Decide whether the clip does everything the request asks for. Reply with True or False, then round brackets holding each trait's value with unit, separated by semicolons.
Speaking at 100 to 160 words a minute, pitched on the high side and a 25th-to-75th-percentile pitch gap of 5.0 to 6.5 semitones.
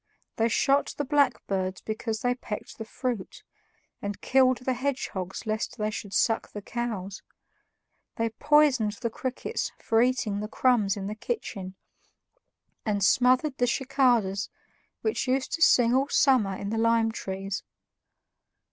False (140 wpm; 230 Hz; 3.9 semitones)